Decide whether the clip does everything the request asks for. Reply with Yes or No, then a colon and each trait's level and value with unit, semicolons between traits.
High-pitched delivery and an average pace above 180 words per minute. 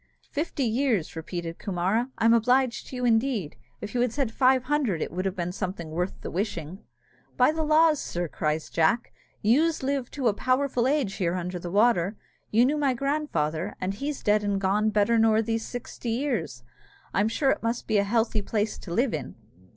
Yes: high, 225 Hz; average, 195 wpm